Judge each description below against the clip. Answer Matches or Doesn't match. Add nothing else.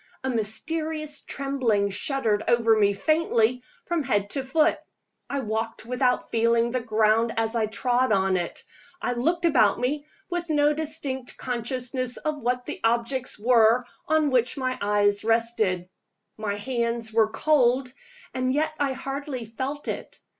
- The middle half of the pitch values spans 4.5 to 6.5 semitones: Doesn't match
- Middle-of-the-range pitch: Doesn't match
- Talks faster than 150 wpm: Doesn't match